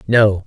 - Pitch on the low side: Yes, low, 105 Hz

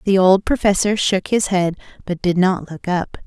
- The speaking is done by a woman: Yes, female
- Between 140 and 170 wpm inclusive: No, average, 200 wpm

